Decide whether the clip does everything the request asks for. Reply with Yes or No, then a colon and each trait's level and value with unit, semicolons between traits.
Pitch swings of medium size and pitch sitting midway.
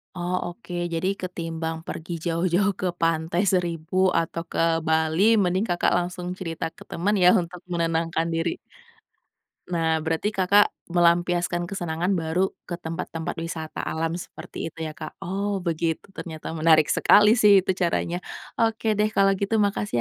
No: narrow, 2.3 semitones; medium, 175 Hz